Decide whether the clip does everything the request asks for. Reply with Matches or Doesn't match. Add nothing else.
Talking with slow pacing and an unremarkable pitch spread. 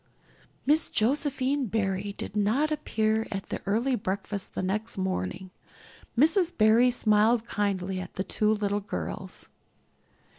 Matches